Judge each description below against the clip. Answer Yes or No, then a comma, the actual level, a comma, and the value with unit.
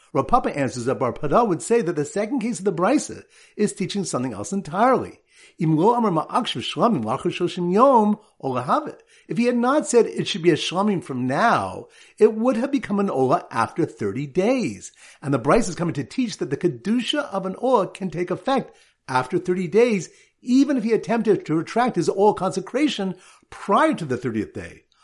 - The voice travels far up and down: Yes, wide, 5.8 semitones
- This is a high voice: Yes, high, 200 Hz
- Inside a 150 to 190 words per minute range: Yes, average, 175 wpm